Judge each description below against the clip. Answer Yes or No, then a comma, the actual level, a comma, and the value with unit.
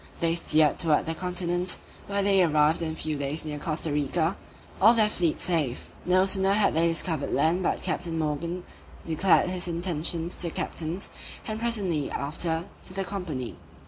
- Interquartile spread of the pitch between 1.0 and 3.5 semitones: Yes, average, 2.9 semitones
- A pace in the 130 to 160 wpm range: No, average, 175 wpm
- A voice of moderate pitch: Yes, medium, 170 Hz